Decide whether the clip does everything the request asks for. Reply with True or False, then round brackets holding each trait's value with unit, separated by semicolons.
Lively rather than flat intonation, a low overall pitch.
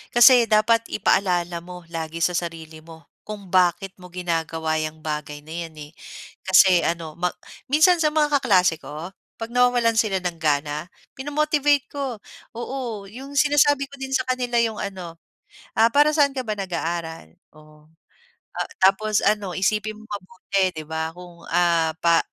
False (6.7 semitones; 190 Hz)